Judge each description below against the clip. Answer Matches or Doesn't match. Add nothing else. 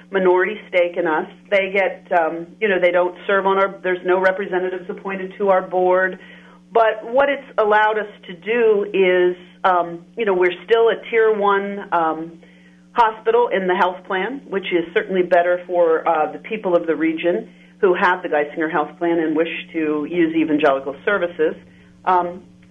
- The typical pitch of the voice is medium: Matches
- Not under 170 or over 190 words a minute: Matches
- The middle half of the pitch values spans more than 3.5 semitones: Doesn't match